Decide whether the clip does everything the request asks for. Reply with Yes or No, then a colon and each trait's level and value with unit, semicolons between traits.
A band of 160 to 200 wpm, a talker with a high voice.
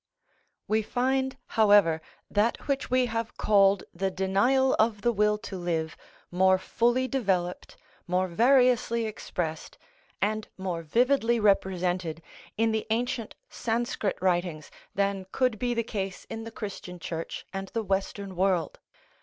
No: slow, 135 wpm; high, 205 Hz